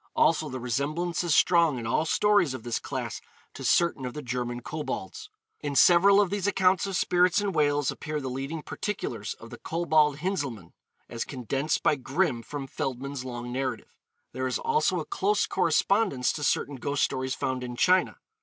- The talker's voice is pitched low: No, medium, 145 Hz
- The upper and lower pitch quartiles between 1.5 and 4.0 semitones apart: No, wide, 5.4 semitones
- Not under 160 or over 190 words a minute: Yes, average, 180 wpm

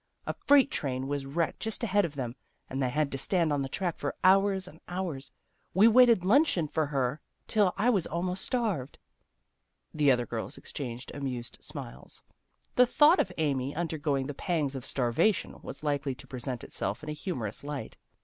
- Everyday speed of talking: Yes, average, 180 wpm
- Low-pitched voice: No, medium, 150 Hz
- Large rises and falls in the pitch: Yes, wide, 5.9 semitones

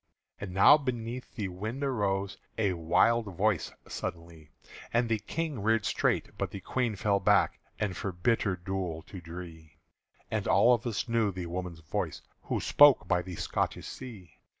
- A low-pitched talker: Yes, low, 100 Hz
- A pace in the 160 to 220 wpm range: Yes, average, 165 wpm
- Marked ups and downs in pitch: No, average, 4.5 semitones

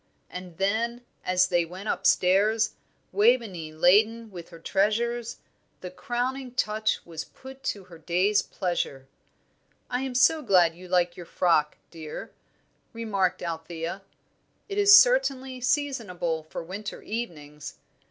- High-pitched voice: Yes, high, 195 Hz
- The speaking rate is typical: No, slow, 125 wpm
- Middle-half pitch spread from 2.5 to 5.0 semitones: No, wide, 5.5 semitones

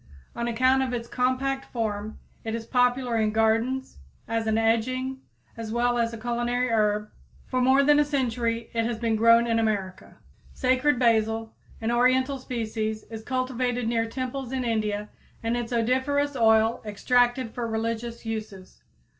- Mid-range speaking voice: No, high, 235 Hz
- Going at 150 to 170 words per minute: Yes, average, 165 wpm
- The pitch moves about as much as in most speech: No, narrow, 2.3 semitones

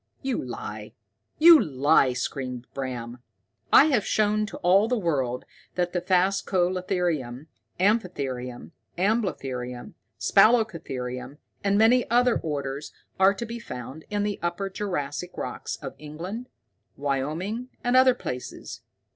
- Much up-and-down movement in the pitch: Yes, wide, 7.7 semitones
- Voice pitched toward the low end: No, medium, 175 Hz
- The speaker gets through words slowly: Yes, slow, 115 wpm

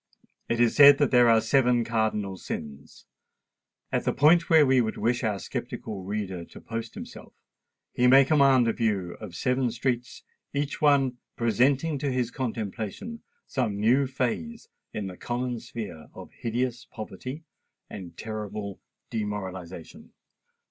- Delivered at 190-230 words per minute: No, average, 140 wpm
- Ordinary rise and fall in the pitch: Yes, average, 4.0 semitones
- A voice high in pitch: No, low, 115 Hz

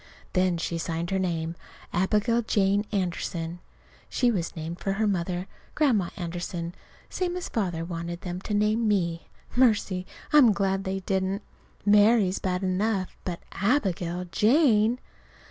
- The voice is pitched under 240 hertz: Yes, high, 190 Hz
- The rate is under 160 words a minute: Yes, average, 140 wpm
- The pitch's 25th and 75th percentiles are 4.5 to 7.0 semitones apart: No, average, 3.4 semitones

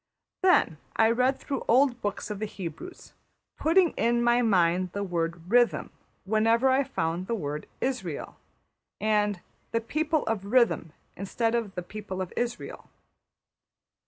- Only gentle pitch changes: No, average, 4.6 semitones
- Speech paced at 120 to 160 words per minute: Yes, average, 145 wpm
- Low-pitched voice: No, high, 220 Hz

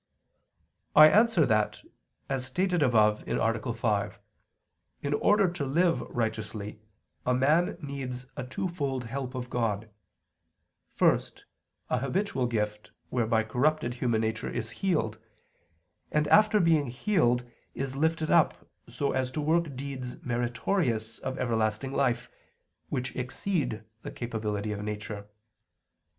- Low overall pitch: Yes, low, 125 Hz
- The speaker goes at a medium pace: No, slow, 120 wpm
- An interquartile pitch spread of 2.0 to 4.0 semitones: No, average, 5.2 semitones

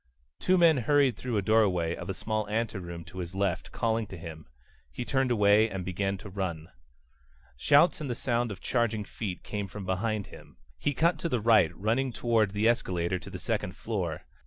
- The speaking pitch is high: No, low, 105 Hz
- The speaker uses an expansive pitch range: No, average, 4.1 semitones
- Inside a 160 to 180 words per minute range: No, average, 195 wpm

